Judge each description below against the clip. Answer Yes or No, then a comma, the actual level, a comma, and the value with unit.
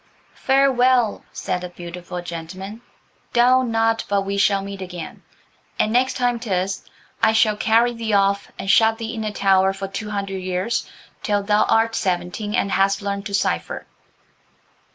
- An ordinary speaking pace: Yes, average, 160 wpm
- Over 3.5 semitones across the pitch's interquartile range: No, average, 2.7 semitones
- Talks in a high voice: Yes, high, 200 Hz